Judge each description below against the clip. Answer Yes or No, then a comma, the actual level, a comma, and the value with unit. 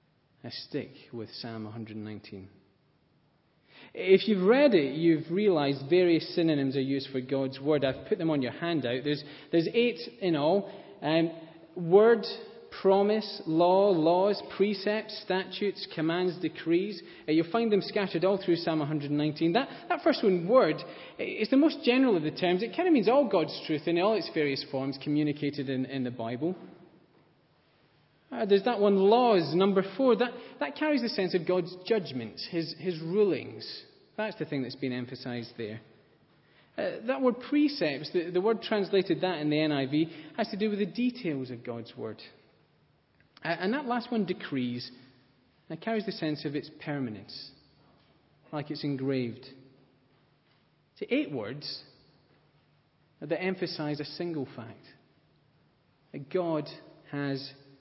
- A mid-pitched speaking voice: Yes, medium, 160 Hz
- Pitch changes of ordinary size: No, wide, 6.1 semitones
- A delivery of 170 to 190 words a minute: No, average, 160 wpm